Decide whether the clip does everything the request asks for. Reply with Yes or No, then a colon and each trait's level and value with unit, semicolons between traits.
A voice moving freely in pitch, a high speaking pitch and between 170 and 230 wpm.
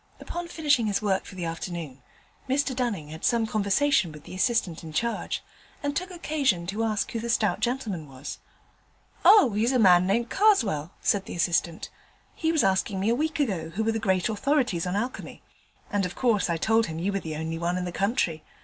Yes: wide, 5.9 semitones; high, 205 Hz; fast, 205 wpm